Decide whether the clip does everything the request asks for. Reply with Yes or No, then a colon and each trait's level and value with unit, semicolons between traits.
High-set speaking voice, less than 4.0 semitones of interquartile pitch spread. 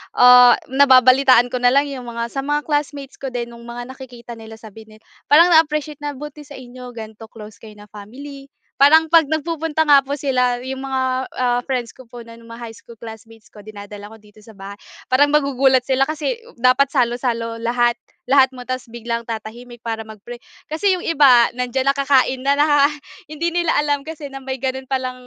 Yes: very high, 255 Hz; average, 3.3 semitones